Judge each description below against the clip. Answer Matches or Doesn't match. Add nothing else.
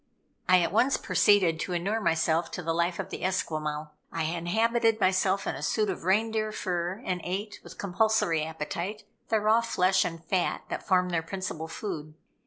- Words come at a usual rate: Matches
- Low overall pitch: Doesn't match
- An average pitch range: Matches